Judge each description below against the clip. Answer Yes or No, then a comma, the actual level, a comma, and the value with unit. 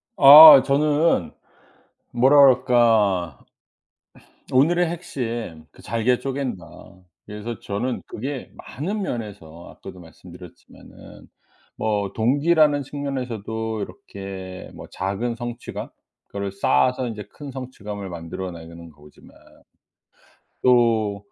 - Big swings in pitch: Yes, wide, 5.7 semitones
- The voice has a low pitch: Yes, low, 115 Hz